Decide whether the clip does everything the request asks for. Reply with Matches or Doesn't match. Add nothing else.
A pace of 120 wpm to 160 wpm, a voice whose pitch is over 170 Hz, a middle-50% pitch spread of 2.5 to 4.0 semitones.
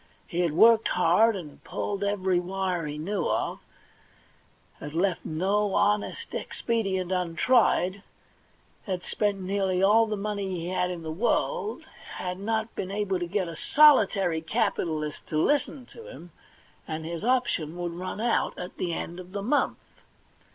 Matches